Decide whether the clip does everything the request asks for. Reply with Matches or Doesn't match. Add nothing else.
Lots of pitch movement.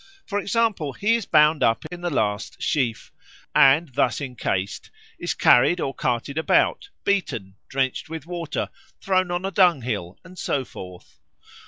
Matches